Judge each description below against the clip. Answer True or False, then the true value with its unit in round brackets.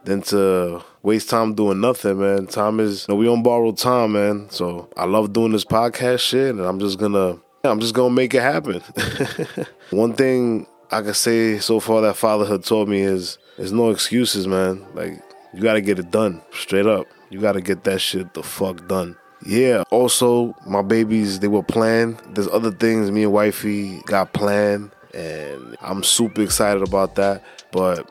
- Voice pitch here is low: True (105 Hz)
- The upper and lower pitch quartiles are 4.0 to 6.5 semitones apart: False (2.6 semitones)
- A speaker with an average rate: True (190 wpm)